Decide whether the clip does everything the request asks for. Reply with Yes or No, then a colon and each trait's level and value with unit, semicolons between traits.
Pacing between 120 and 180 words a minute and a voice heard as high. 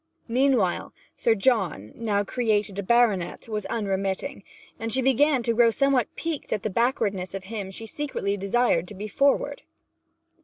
Yes: average, 155 wpm; high, 220 Hz